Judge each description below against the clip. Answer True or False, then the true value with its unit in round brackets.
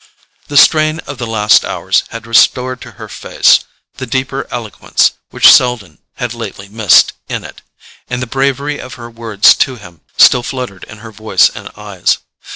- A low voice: True (120 Hz)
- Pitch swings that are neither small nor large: True (3.6 semitones)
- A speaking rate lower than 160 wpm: False (170 wpm)